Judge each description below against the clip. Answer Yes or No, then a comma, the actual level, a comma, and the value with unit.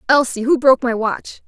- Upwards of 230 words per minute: No, fast, 205 wpm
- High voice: Yes, very high, 250 Hz